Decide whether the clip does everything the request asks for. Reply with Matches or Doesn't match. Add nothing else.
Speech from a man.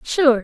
Doesn't match